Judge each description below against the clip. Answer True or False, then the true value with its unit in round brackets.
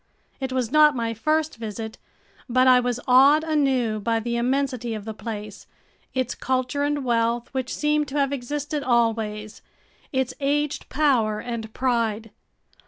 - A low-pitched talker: False (250 Hz)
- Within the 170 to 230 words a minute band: False (150 wpm)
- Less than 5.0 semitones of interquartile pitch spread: True (3.6 semitones)